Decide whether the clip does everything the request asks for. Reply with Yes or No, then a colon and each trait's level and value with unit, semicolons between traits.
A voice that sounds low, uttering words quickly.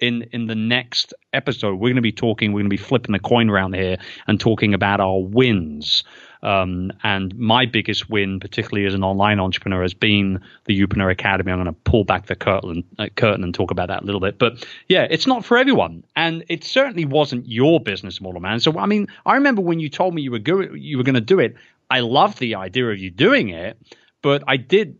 Yes: low, 110 Hz; fast, 230 wpm